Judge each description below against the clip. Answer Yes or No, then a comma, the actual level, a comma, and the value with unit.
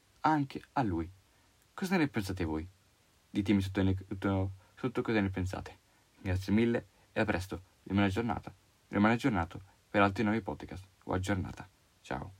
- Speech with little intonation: Yes, narrow, 2.3 semitones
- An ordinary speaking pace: Yes, average, 155 wpm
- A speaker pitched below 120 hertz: Yes, low, 100 Hz